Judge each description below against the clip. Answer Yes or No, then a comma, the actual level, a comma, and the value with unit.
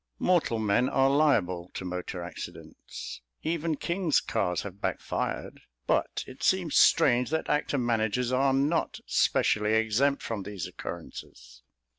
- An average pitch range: No, wide, 6.1 semitones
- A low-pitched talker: Yes, low, 120 Hz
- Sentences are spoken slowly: Yes, slow, 130 wpm